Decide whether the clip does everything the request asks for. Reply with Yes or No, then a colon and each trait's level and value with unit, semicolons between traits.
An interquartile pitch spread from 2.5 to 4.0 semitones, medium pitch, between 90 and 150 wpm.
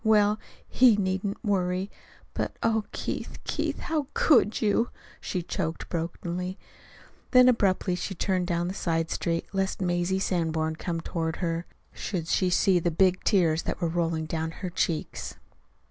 Yes: average, 3.0 semitones; medium, 180 Hz; average, 145 wpm